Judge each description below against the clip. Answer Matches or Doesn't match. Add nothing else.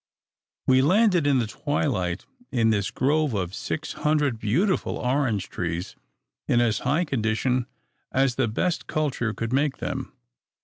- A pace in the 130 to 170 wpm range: Matches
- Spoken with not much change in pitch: Doesn't match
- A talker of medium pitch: Doesn't match